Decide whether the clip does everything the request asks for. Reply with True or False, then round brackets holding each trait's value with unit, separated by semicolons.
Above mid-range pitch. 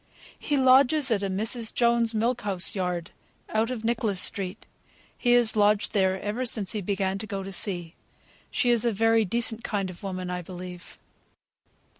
True (210 Hz)